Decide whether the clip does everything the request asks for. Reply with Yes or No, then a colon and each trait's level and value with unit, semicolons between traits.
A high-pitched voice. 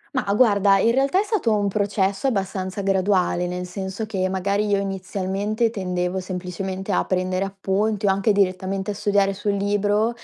Yes: high, 195 Hz